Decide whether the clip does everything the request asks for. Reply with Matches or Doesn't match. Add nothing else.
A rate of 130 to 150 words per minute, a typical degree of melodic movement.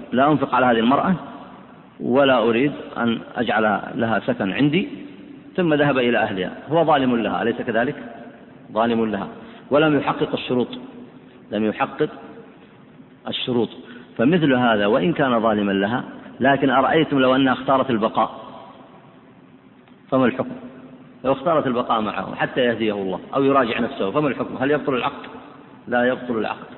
Matches